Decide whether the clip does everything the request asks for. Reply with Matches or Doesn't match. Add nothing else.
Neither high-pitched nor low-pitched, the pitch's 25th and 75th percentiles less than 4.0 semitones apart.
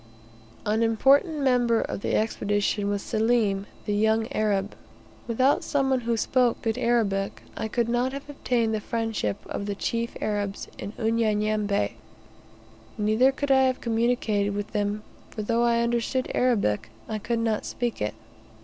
Doesn't match